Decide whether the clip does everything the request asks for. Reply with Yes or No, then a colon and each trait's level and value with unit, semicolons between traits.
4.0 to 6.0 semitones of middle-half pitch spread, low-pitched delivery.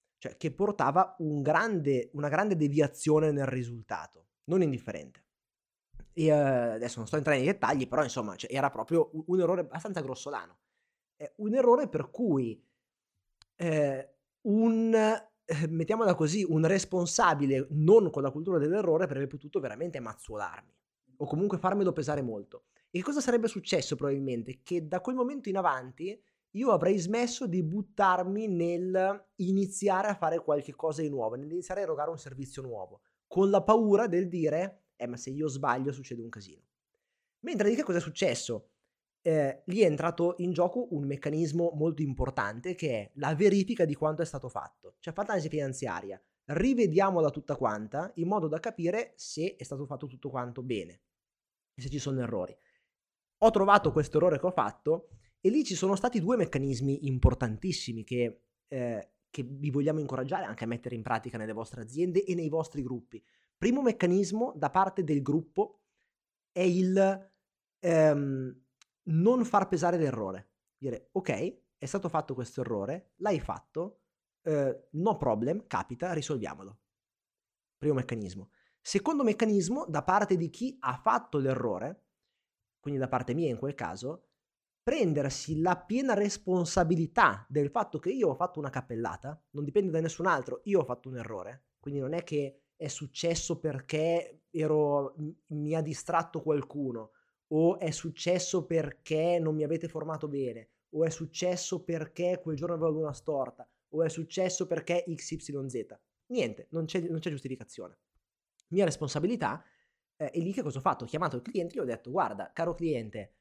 No: average, 5.2 semitones; medium, 160 Hz